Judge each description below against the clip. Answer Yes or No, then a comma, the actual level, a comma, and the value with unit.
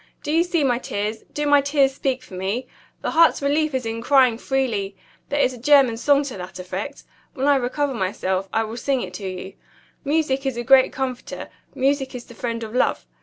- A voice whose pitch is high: Yes, very high, 255 Hz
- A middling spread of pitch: Yes, average, 4.0 semitones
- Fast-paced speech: Yes, fast, 215 wpm